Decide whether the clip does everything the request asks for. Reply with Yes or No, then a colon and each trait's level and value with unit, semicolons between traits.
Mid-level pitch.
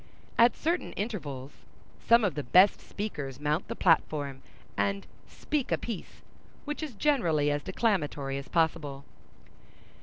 Yes: medium, 165 Hz